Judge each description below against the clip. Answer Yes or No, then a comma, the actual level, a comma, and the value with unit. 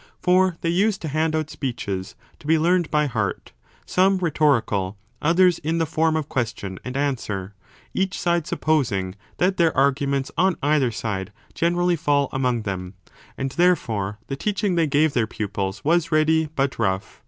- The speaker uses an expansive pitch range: Yes, wide, 6.6 semitones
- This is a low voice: No, medium, 150 Hz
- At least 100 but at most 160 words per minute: No, average, 170 wpm